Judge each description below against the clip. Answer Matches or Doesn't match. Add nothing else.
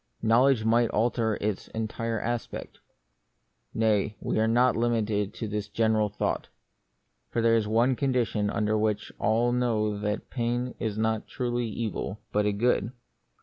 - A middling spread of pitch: Doesn't match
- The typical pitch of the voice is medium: Doesn't match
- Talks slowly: Doesn't match